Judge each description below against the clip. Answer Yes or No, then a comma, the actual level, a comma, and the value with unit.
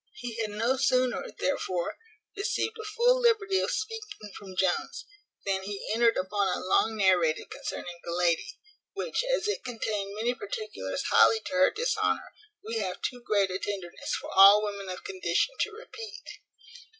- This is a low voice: No, high, 225 Hz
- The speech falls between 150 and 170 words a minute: Yes, average, 160 wpm